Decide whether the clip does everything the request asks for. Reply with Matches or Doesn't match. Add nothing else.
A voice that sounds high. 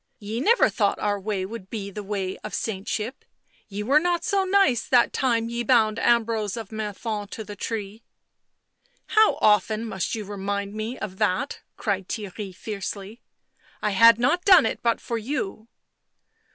Matches